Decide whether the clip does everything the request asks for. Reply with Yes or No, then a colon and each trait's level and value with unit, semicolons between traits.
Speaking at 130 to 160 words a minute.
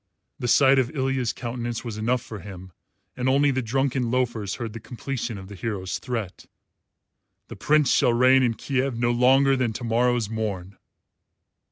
No: average, 175 wpm